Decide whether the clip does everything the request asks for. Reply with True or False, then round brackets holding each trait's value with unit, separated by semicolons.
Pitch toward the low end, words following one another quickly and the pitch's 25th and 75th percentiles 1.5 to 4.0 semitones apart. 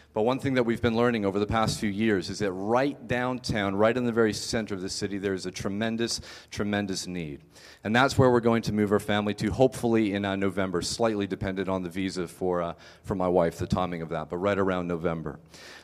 True (100 Hz; 235 wpm; 3.7 semitones)